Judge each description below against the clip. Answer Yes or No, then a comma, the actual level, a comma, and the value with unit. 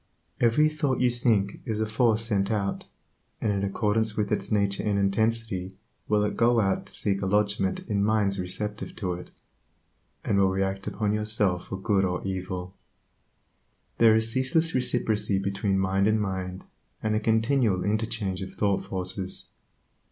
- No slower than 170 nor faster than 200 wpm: No, average, 160 wpm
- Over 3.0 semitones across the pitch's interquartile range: No, narrow, 2.4 semitones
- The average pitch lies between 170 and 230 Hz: No, low, 105 Hz